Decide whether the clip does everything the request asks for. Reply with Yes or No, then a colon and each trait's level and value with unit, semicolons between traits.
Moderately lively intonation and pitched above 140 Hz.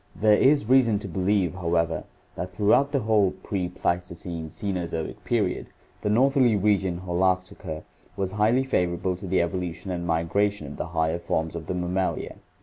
No: average, 3.2 semitones; very low, 90 Hz